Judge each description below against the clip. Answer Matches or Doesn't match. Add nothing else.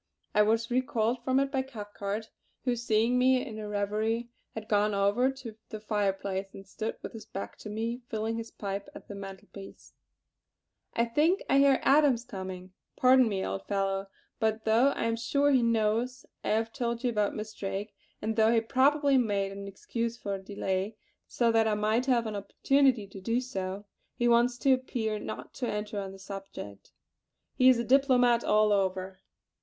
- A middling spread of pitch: Matches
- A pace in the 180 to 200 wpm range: Matches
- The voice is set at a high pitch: Matches